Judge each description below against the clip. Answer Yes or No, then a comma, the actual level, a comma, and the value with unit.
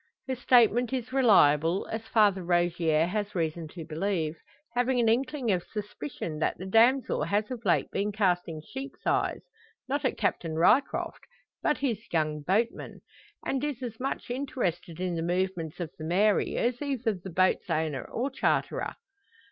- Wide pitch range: Yes, wide, 6.4 semitones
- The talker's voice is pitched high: Yes, high, 200 Hz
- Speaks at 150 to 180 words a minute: Yes, average, 160 wpm